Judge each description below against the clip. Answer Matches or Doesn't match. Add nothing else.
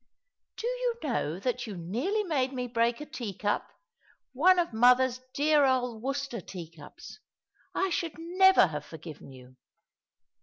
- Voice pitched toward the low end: Doesn't match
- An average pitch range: Doesn't match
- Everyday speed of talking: Matches